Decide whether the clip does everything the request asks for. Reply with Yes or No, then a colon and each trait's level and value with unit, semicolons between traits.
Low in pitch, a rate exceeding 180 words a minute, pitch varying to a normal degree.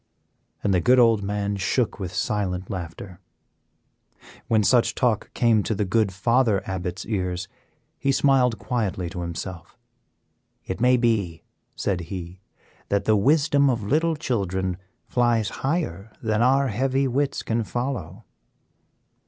No: low, 105 Hz; slow, 135 wpm; average, 5.0 semitones